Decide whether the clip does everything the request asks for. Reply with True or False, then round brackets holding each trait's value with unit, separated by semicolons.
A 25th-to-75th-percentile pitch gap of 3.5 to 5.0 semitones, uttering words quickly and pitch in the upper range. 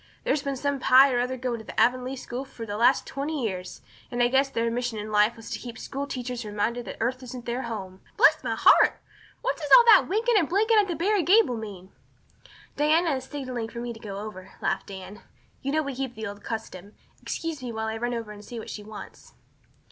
True (4.0 semitones; 230 wpm; 245 Hz)